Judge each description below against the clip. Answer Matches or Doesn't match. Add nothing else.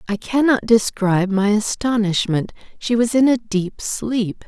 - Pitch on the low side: Doesn't match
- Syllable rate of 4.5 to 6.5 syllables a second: Doesn't match